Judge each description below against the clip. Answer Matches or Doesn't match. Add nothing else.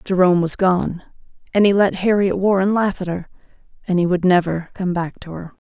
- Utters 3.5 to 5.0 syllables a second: Doesn't match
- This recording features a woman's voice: Matches